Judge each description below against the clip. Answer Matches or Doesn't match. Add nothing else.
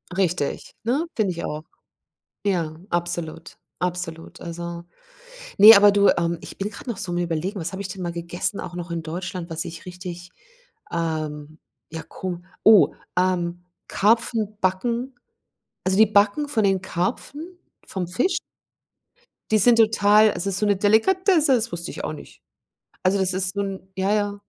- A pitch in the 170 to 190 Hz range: Matches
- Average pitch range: Matches